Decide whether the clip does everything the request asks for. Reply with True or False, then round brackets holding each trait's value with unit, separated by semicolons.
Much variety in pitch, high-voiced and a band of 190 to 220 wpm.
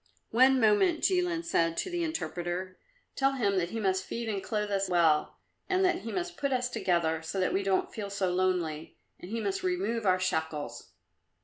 True (7.0 semitones; 200 Hz; 195 wpm)